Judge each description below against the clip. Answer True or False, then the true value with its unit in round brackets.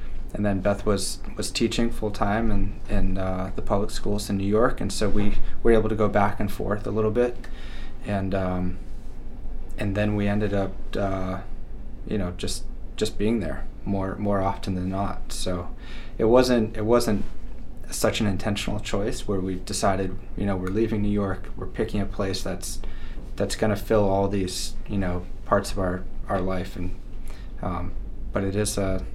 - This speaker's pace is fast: False (185 wpm)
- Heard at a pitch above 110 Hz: False (100 Hz)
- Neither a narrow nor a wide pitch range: False (2.2 semitones)